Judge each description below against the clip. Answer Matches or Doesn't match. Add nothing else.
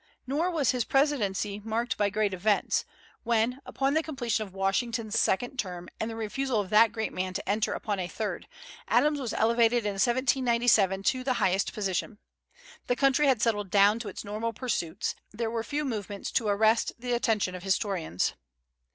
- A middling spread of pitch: Matches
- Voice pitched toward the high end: Matches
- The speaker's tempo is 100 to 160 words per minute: Doesn't match